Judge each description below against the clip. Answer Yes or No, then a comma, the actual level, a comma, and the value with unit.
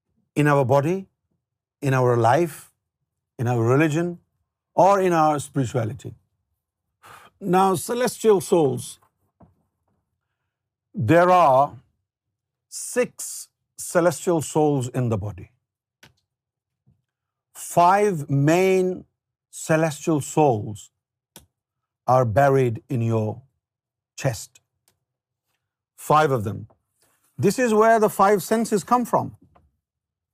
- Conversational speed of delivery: No, slow, 80 wpm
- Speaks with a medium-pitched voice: No, low, 130 Hz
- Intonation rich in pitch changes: Yes, wide, 6.4 semitones